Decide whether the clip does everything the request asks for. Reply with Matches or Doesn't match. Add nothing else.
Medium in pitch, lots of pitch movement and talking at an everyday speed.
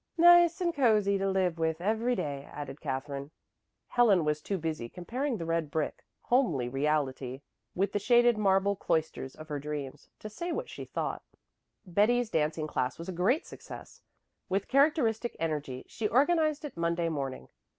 Matches